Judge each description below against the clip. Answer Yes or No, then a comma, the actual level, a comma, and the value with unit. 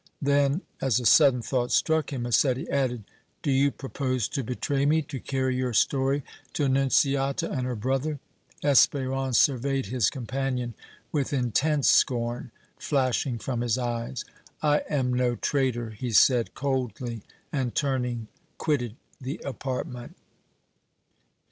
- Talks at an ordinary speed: No, slow, 130 wpm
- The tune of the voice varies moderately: No, narrow, 2.2 semitones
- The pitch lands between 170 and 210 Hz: No, low, 130 Hz